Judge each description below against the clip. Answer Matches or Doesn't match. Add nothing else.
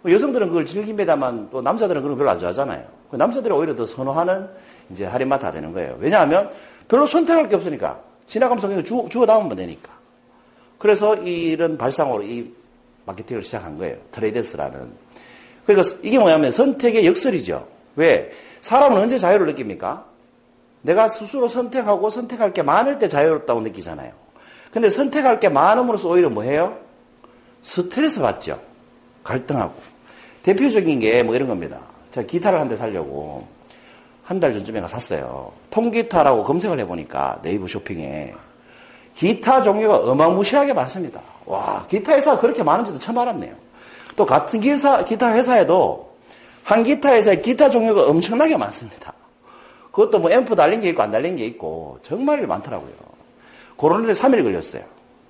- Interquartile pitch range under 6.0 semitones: Doesn't match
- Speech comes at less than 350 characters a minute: Doesn't match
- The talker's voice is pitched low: Doesn't match